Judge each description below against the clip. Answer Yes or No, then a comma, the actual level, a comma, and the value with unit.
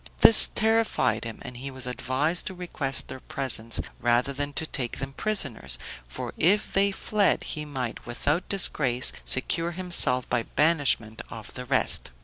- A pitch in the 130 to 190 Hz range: Yes, low, 135 Hz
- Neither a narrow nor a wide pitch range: No, wide, 5.9 semitones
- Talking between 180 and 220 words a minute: No, average, 155 wpm